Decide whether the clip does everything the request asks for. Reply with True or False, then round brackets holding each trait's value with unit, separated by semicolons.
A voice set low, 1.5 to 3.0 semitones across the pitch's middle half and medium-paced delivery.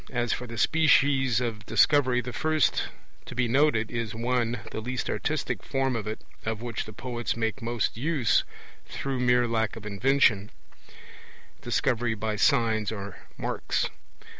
True (120 Hz; 2.4 semitones; 150 wpm)